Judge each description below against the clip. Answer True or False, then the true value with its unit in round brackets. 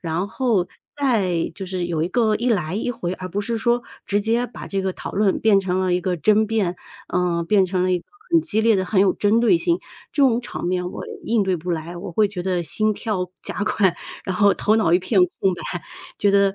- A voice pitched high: True (195 Hz)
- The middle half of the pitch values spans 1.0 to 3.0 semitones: False (3.4 semitones)